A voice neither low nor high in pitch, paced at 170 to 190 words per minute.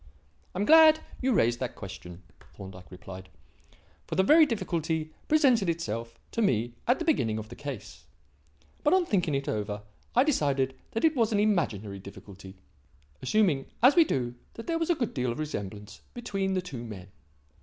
Yes: medium, 150 Hz; average, 175 wpm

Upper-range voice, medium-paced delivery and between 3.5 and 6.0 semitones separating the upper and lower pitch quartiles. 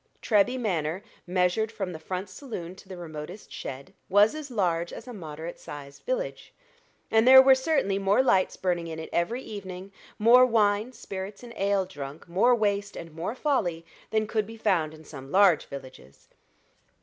Yes: high, 195 Hz; average, 175 wpm; average, 4.9 semitones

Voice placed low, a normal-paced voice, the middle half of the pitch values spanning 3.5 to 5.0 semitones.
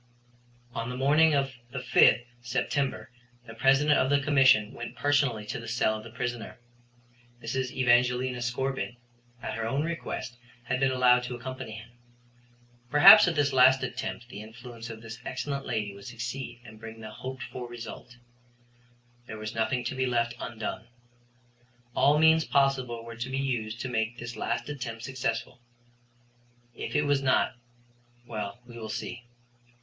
No: low, 125 Hz; average, 160 wpm; narrow, 2.6 semitones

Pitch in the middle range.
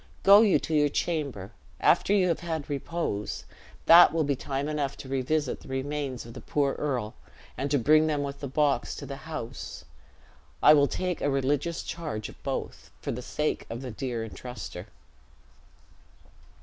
Yes: medium, 145 Hz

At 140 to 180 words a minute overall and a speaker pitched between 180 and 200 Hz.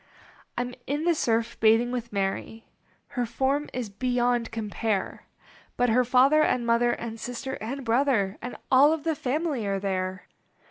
No: average, 160 wpm; high, 240 Hz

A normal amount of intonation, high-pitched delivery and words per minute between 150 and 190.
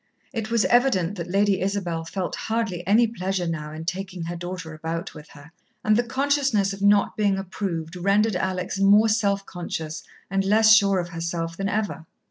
Yes: average, 3.6 semitones; high, 195 Hz; average, 180 wpm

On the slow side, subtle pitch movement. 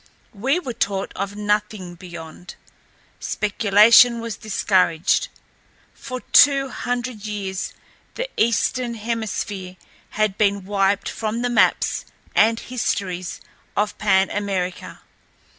No: slow, 105 wpm; average, 3.3 semitones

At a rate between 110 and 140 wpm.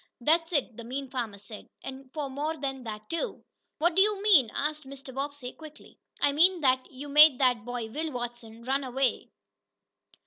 No: average, 180 wpm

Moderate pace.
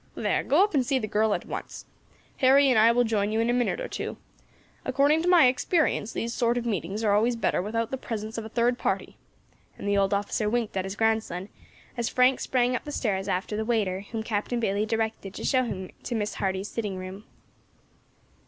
No: fast, 220 wpm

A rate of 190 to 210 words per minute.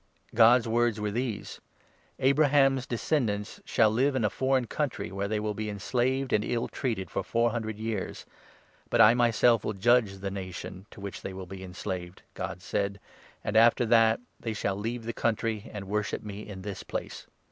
Yes: average, 195 wpm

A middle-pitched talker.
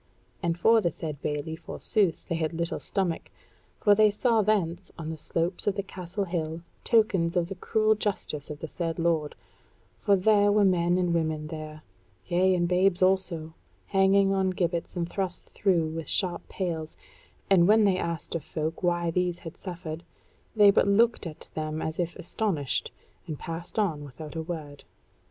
Yes: medium, 175 Hz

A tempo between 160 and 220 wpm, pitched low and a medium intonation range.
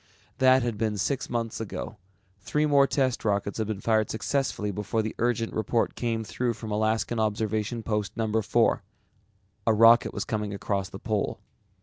No: average, 165 wpm; low, 110 Hz; narrow, 2.0 semitones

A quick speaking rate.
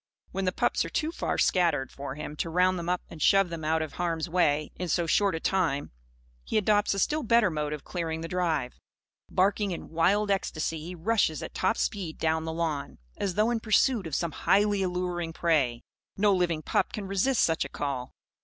Yes: fast, 210 wpm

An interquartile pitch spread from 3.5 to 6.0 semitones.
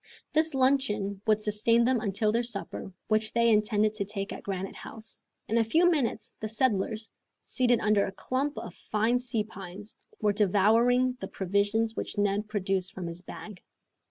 No: average, 2.7 semitones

